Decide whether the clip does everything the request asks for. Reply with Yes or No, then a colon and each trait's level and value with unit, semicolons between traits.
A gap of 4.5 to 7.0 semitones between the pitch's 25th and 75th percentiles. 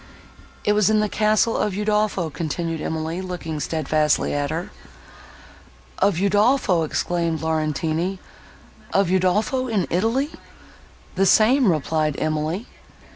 Yes: average, 4.8 semitones